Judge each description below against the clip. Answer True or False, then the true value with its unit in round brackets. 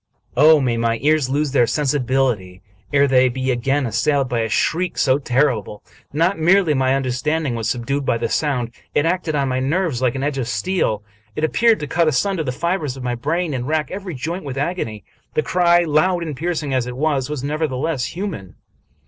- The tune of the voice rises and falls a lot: False (4.1 semitones)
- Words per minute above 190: True (200 wpm)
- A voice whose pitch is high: False (140 Hz)